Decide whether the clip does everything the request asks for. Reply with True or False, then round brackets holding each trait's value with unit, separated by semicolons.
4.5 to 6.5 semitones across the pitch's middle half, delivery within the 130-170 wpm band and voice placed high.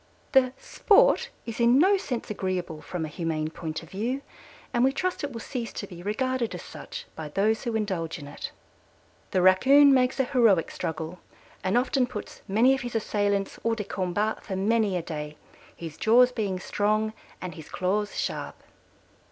False (5.4 semitones; 180 wpm; 210 Hz)